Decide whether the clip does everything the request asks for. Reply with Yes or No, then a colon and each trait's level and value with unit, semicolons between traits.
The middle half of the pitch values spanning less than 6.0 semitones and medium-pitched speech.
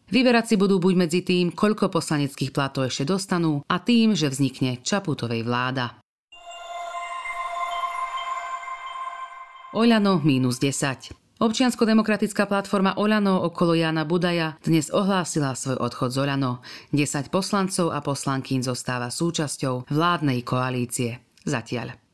No: wide, 8.1 semitones; medium, 170 Hz